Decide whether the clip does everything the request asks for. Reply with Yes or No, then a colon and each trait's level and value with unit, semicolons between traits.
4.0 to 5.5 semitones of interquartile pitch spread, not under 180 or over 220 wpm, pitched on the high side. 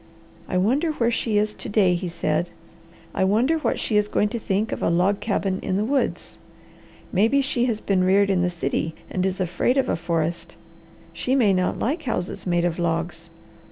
Yes: average, 4.4 semitones; average, 200 wpm; high, 195 Hz